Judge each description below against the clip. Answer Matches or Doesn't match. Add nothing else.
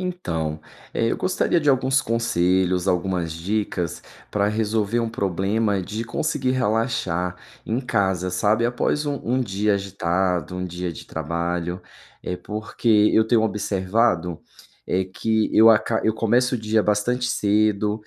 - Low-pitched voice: Matches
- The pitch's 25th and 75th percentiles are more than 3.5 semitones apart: Matches